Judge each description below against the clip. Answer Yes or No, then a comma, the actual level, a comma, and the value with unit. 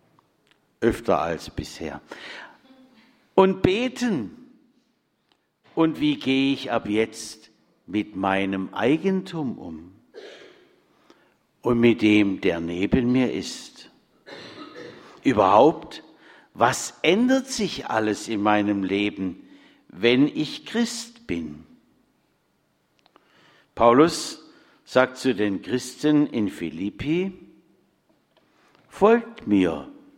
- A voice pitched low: No, medium, 150 Hz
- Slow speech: Yes, slow, 85 wpm